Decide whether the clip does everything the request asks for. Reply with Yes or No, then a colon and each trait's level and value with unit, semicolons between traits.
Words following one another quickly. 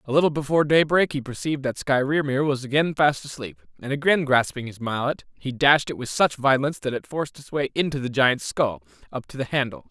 Yes: fast, 220 wpm